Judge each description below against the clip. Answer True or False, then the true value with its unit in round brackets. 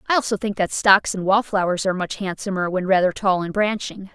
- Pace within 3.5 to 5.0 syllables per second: False (5.8 syllables/s)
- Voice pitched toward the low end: False (195 Hz)